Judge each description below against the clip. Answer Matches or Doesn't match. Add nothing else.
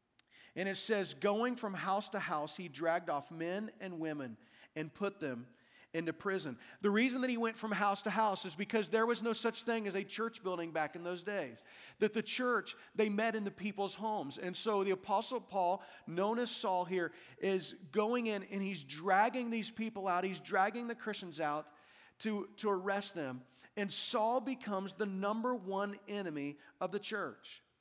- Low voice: Doesn't match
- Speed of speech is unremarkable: Matches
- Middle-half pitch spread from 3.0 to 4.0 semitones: Matches